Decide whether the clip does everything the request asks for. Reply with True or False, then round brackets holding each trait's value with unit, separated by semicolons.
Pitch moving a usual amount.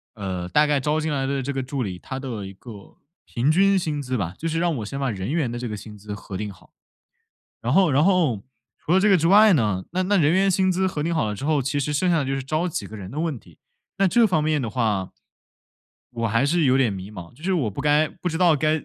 False (7.1 semitones)